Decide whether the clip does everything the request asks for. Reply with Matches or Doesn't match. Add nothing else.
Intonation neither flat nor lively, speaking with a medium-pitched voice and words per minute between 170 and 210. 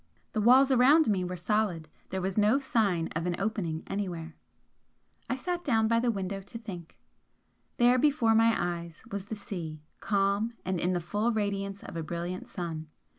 Doesn't match